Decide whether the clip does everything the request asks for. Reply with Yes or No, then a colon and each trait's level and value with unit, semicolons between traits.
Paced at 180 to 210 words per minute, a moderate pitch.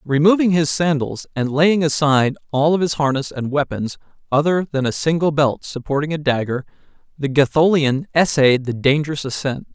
No: average, 160 wpm; medium, 145 Hz